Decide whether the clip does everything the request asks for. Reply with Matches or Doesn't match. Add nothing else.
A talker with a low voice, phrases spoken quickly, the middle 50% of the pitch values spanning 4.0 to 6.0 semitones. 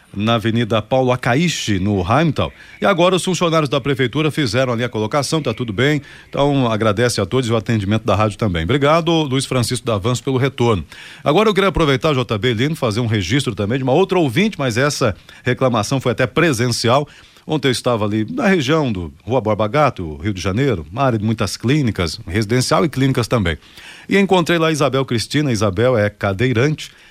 Matches